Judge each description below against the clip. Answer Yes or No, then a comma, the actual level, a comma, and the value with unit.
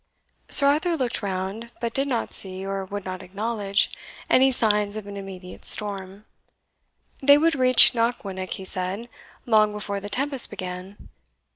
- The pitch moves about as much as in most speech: Yes, average, 3.8 semitones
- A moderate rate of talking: Yes, average, 150 wpm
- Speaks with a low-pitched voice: No, high, 205 Hz